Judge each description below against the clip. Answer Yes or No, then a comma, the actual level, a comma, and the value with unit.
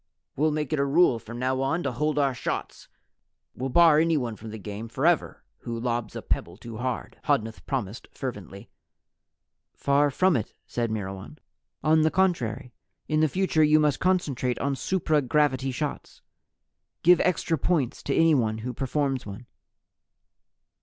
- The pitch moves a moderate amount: Yes, average, 4.8 semitones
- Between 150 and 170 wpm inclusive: Yes, average, 155 wpm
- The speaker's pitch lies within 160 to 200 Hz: No, low, 135 Hz